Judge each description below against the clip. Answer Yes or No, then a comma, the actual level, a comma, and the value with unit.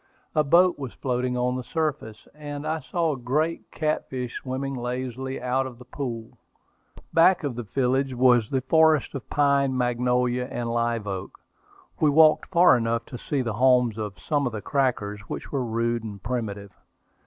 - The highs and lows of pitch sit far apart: No, average, 3.3 semitones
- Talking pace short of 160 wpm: No, average, 170 wpm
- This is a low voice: Yes, low, 125 Hz